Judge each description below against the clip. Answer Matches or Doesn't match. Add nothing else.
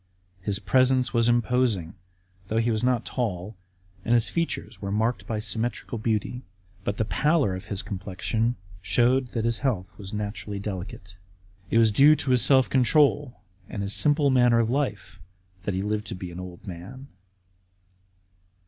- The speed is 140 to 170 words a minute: Matches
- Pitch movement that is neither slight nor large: Matches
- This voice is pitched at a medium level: Doesn't match